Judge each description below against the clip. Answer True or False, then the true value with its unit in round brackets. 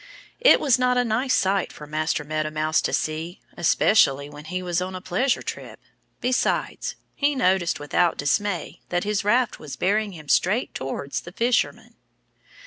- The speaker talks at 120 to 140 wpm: False (165 wpm)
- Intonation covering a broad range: True (6.0 semitones)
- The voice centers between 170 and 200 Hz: True (185 Hz)